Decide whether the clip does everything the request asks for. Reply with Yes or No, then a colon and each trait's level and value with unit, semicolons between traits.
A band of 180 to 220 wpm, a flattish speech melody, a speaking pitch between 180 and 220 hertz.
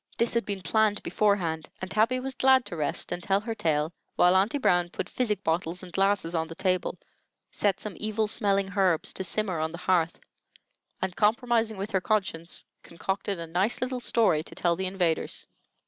No: average, 190 wpm; average, 3.8 semitones; high, 190 Hz